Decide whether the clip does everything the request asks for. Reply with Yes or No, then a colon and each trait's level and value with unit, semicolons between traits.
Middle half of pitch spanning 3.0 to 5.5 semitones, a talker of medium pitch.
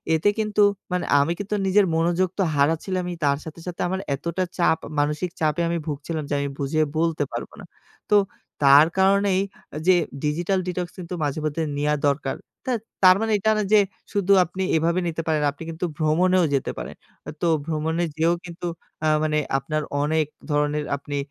Yes: average, 3.3 semitones; medium, 165 Hz